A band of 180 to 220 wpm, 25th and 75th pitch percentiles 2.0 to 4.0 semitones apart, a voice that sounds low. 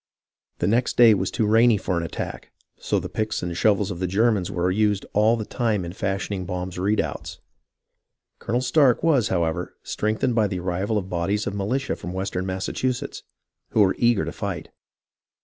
Yes: average, 185 wpm; average, 3.4 semitones; low, 100 Hz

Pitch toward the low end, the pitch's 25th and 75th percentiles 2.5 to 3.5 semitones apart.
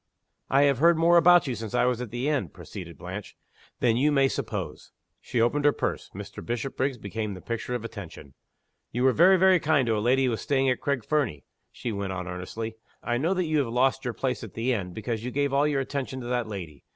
No: low, 125 Hz; average, 4.1 semitones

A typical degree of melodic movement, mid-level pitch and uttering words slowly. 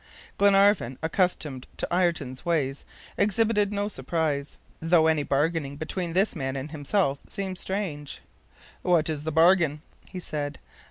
Yes: average, 4.7 semitones; medium, 160 Hz; slow, 130 wpm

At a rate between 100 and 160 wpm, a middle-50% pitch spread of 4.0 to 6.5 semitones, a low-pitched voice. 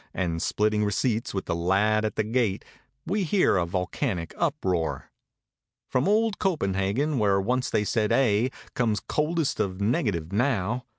Yes: average, 150 wpm; average, 5.0 semitones; low, 105 Hz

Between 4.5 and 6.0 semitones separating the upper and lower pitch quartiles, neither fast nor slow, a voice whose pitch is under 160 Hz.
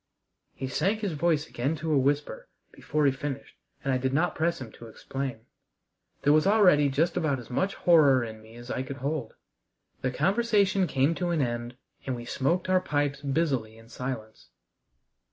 Yes: average, 4.8 semitones; average, 185 wpm; medium, 140 Hz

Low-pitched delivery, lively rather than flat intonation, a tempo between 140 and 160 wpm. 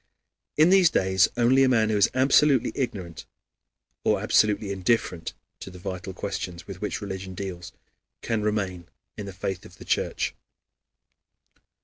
No: low, 100 Hz; average, 3.9 semitones; average, 145 wpm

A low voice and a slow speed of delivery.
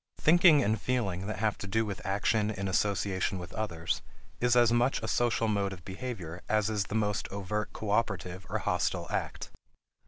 No: low, 105 Hz; average, 180 wpm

